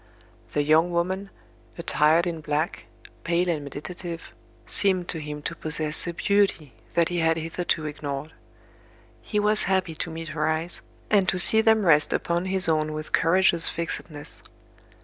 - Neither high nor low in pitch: Yes, medium, 165 Hz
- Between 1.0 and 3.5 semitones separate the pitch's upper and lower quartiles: Yes, average, 2.9 semitones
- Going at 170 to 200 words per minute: No, average, 155 wpm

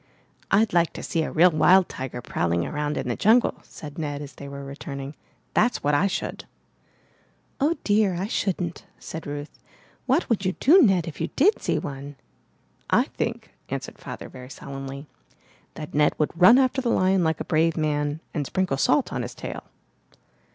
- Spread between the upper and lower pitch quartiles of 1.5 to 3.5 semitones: No, average, 5.1 semitones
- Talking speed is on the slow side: No, average, 180 wpm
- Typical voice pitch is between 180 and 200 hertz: No, medium, 160 Hz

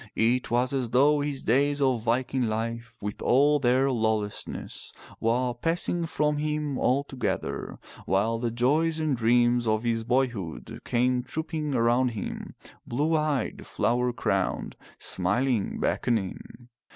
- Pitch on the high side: No, low, 125 Hz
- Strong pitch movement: No, average, 3.4 semitones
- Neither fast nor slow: No, slow, 125 wpm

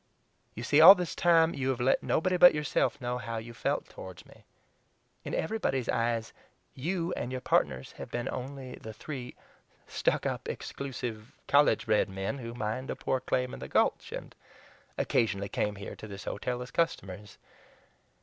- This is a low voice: Yes, low, 125 Hz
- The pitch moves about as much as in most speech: Yes, average, 4.4 semitones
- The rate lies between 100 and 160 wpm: No, average, 170 wpm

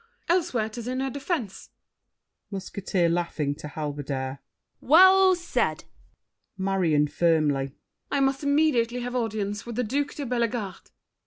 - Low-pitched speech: No, high, 220 Hz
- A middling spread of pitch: No, wide, 8.2 semitones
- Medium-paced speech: No, slow, 125 wpm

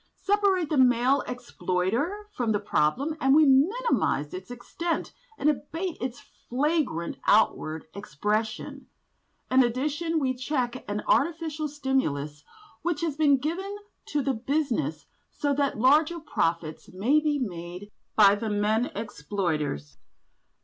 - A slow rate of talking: Yes, slow, 125 wpm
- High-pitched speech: Yes, very high, 260 Hz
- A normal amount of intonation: No, wide, 6.8 semitones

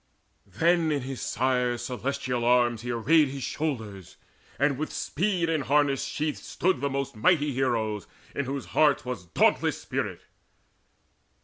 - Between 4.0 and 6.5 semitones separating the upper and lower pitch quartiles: No, average, 3.5 semitones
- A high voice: No, low, 135 Hz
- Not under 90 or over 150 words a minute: Yes, average, 140 wpm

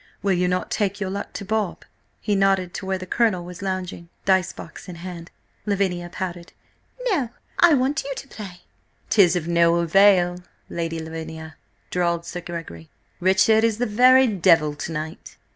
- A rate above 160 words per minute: Yes, average, 170 wpm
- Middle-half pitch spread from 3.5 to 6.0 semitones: No, average, 2.9 semitones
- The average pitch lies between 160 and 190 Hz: Yes, medium, 185 Hz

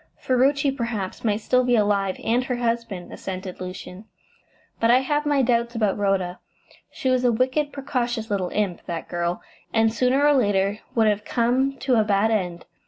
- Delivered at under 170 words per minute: No, average, 175 wpm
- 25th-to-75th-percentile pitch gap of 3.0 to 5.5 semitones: Yes, average, 4.3 semitones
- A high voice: Yes, high, 230 Hz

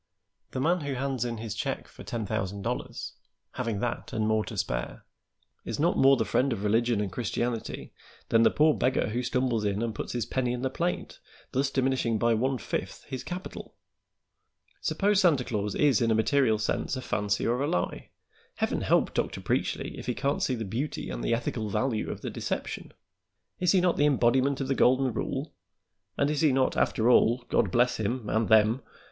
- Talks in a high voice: No, low, 120 Hz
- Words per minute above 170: Yes, average, 200 wpm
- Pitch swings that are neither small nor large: Yes, average, 3.5 semitones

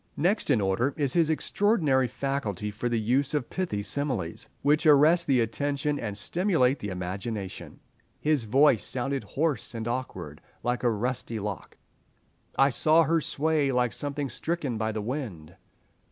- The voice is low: Yes, low, 130 Hz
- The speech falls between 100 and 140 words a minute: No, average, 155 wpm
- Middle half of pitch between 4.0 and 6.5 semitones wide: Yes, average, 5.2 semitones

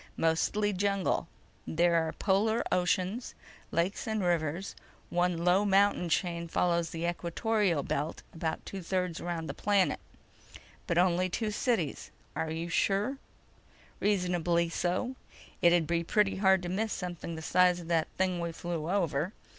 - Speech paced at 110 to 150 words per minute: Yes, average, 145 wpm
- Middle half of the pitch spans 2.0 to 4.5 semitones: Yes, narrow, 2.6 semitones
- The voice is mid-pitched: Yes, medium, 180 Hz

